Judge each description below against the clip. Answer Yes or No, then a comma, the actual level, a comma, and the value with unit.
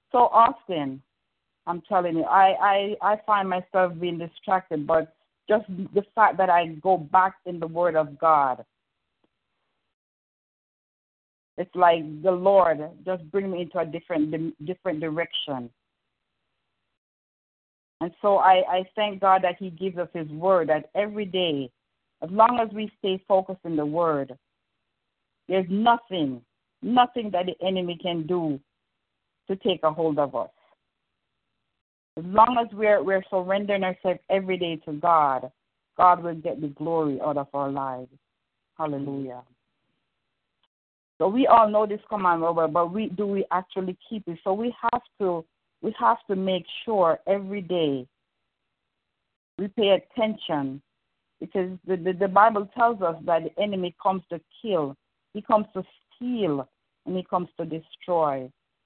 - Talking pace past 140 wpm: Yes, average, 150 wpm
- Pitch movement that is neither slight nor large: Yes, average, 3.9 semitones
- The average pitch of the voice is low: No, medium, 180 Hz